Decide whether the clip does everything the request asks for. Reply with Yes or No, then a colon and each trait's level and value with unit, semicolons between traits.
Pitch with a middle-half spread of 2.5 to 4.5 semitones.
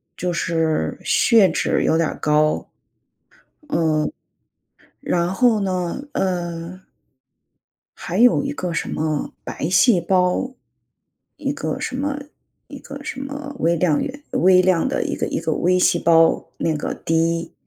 Yes: average, 3.3 semitones